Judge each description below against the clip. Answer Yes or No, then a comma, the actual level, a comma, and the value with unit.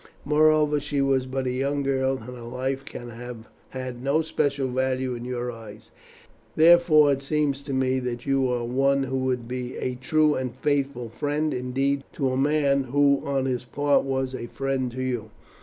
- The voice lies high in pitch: No, low, 130 Hz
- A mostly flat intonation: Yes, narrow, 1.9 semitones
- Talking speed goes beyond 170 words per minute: Yes, average, 190 wpm